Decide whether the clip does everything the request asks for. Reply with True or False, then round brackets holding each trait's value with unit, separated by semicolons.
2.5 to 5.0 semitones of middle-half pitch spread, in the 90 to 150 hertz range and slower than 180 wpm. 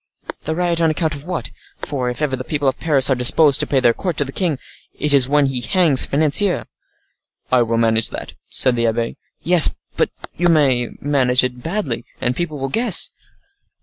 False (4.5 semitones; 140 Hz; 200 wpm)